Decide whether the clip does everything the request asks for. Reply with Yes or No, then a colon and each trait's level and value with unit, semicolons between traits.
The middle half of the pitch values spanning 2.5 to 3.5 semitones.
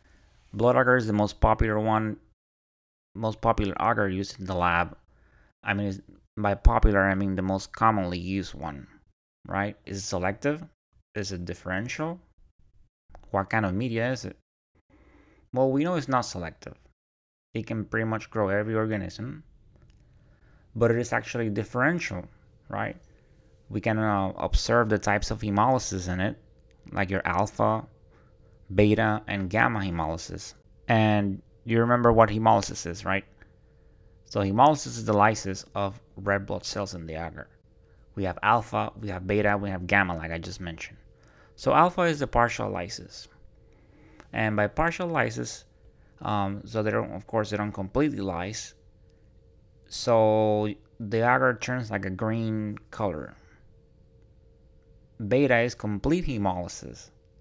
Yes: average, 2.9 semitones